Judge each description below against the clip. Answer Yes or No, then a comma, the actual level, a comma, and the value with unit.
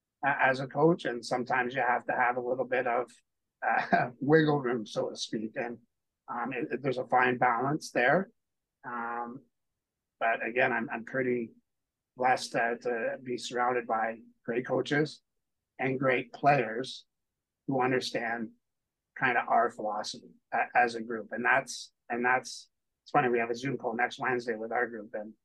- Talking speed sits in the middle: Yes, average, 165 wpm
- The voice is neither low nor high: No, low, 125 Hz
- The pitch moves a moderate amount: No, narrow, 1.9 semitones